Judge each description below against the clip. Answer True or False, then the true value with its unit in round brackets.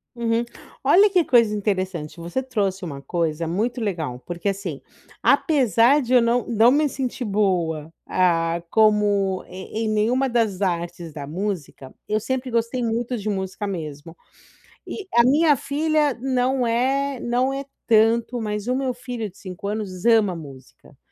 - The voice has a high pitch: True (215 Hz)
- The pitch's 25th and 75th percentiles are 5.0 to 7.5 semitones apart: True (5.4 semitones)